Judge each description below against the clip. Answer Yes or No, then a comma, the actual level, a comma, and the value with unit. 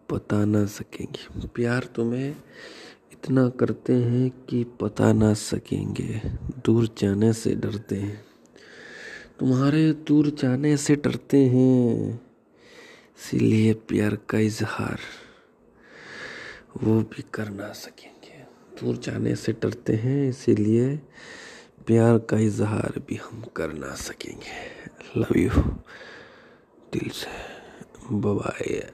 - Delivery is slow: Yes, slow, 105 wpm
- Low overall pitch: Yes, low, 115 Hz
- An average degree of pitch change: Yes, average, 3.4 semitones